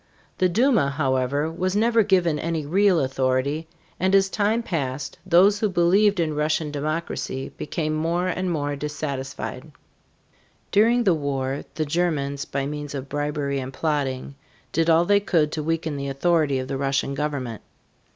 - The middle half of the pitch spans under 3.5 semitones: No, average, 4.1 semitones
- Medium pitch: Yes, medium, 155 Hz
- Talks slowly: No, average, 155 wpm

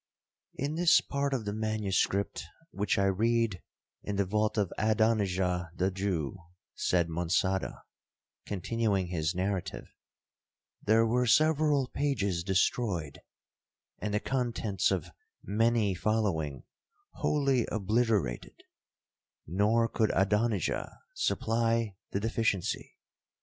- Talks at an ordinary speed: No, slow, 100 wpm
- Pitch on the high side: No, low, 105 Hz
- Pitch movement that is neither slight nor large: Yes, average, 3.4 semitones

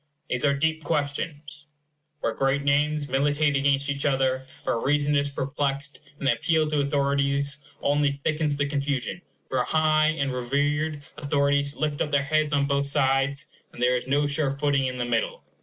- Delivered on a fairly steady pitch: Yes, narrow, 1.2 semitones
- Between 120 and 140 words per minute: No, average, 175 wpm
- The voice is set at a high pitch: No, medium, 140 Hz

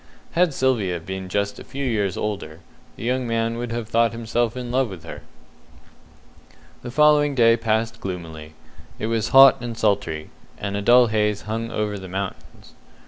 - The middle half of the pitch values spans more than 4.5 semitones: No, average, 3.5 semitones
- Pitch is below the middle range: Yes, low, 115 Hz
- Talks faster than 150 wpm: Yes, average, 170 wpm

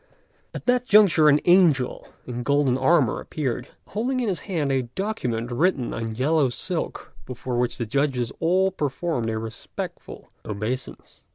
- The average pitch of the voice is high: No, medium, 140 Hz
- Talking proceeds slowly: No, average, 150 wpm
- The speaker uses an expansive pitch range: Yes, wide, 6.3 semitones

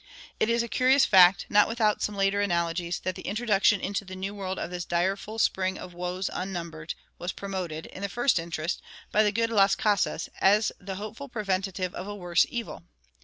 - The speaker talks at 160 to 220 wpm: Yes, average, 195 wpm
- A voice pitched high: Yes, high, 195 Hz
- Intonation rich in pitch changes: No, average, 2.8 semitones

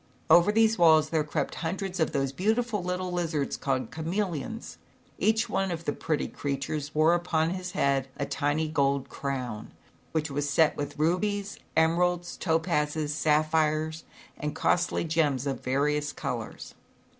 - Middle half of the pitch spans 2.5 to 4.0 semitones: Yes, average, 3.4 semitones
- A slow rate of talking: No, average, 145 wpm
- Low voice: No, medium, 160 Hz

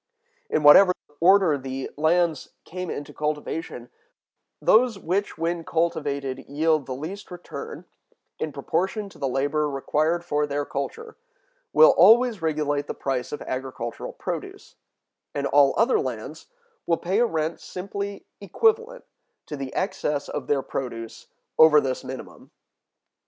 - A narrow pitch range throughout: No, average, 4.7 semitones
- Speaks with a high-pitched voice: No, medium, 155 Hz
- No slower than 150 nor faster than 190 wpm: No, slow, 135 wpm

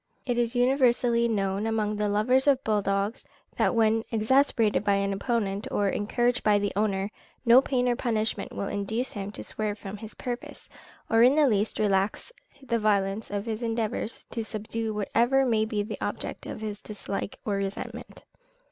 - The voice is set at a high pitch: Yes, high, 220 Hz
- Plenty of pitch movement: No, average, 2.7 semitones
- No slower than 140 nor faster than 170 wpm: No, average, 180 wpm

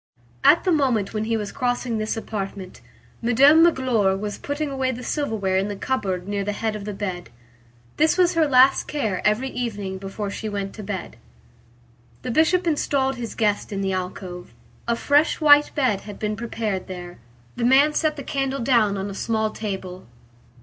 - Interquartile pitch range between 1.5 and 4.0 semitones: No, average, 5.2 semitones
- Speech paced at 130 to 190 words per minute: Yes, average, 185 wpm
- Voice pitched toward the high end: Yes, high, 220 Hz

